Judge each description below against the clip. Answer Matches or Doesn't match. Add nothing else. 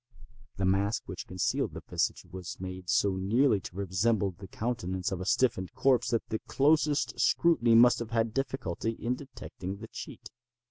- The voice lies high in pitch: Doesn't match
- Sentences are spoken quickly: Doesn't match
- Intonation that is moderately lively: Matches